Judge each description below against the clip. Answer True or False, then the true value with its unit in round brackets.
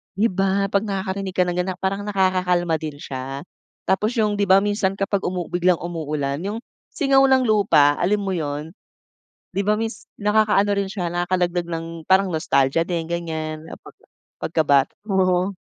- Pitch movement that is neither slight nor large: True (3.3 semitones)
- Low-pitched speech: False (185 Hz)